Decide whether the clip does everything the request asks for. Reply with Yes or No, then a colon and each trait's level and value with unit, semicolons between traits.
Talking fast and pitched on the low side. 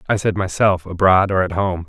Yes: fast, 225 wpm; very low, 95 Hz